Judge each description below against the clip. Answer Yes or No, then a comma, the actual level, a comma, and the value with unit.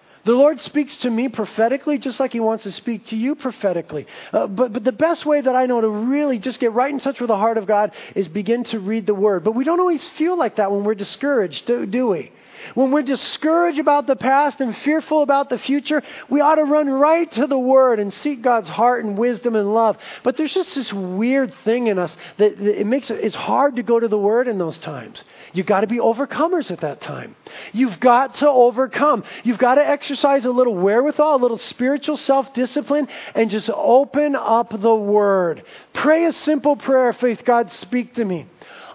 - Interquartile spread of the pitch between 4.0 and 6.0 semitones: Yes, average, 4.3 semitones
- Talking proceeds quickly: Yes, fast, 220 wpm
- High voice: Yes, very high, 250 Hz